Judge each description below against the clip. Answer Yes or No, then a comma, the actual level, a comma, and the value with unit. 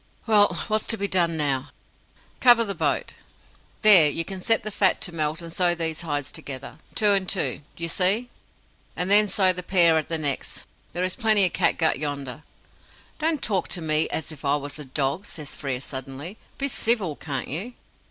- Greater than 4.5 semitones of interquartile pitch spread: Yes, average, 5.3 semitones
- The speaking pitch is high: No, medium, 170 Hz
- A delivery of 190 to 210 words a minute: Yes, average, 195 wpm